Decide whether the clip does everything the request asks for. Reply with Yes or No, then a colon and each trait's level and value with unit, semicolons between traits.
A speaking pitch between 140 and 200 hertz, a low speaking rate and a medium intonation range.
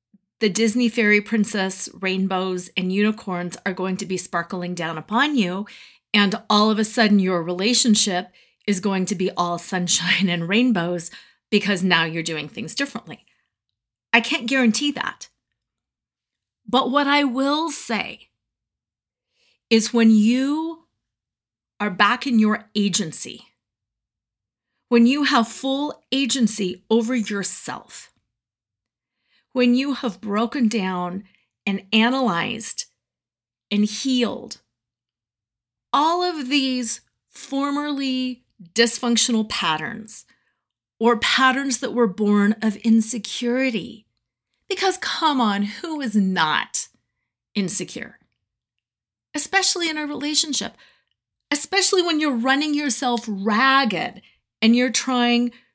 No: high, 225 Hz; slow, 110 wpm; average, 4.8 semitones